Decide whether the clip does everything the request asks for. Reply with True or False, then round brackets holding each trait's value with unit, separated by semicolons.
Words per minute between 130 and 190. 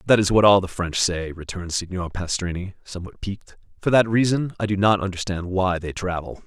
False (205 wpm)